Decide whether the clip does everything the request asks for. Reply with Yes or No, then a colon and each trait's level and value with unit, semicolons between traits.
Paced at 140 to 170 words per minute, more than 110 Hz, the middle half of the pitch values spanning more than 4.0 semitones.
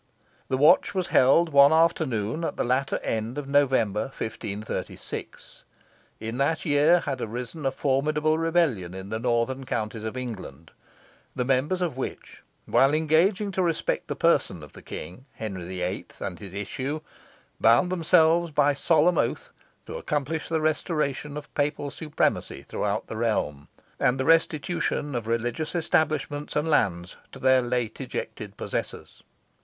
Yes: average, 150 wpm; low, 135 Hz; wide, 5.6 semitones